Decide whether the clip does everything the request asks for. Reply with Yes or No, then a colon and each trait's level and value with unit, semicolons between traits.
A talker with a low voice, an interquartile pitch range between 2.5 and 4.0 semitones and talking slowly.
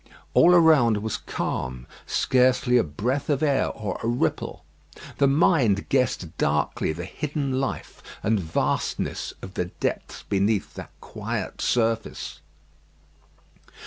No: low, 120 Hz; wide, 5.6 semitones; slow, 120 wpm